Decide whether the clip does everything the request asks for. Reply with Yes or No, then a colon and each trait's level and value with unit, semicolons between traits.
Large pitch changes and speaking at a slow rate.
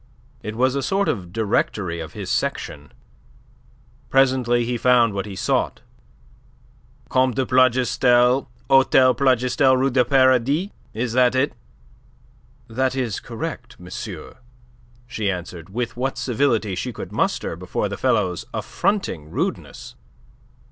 No: average, 3.5 semitones; slow, 125 wpm